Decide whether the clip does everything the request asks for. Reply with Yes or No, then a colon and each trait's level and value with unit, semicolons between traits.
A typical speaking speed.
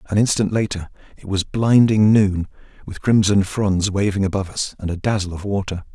Yes: average, 180 wpm